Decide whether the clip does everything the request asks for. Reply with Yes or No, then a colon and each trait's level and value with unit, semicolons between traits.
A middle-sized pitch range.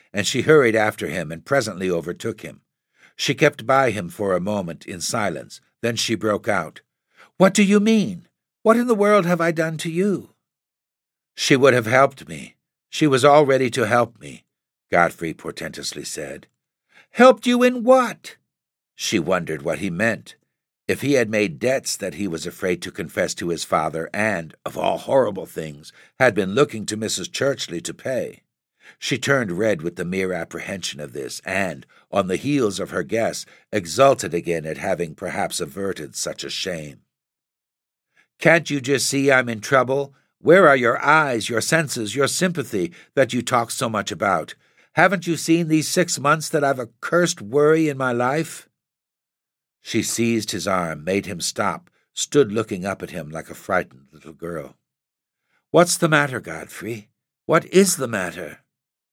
No: wide, 7.8 semitones